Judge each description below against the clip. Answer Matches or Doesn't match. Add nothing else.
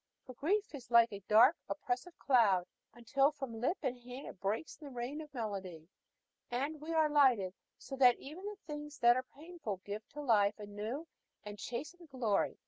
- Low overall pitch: Doesn't match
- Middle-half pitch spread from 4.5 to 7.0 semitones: Matches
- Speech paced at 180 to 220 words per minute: Matches